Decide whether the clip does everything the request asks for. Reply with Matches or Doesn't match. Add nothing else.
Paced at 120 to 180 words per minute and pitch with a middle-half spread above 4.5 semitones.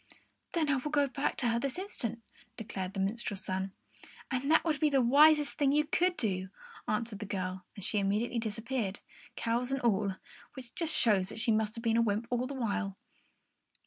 Doesn't match